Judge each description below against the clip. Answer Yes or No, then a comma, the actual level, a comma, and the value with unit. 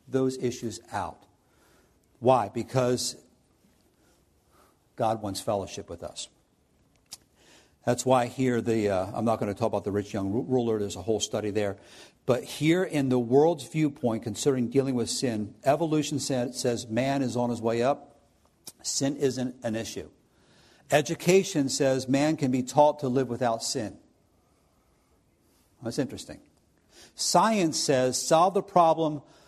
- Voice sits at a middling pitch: No, low, 125 Hz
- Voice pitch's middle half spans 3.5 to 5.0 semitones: Yes, average, 3.9 semitones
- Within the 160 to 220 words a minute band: No, average, 140 wpm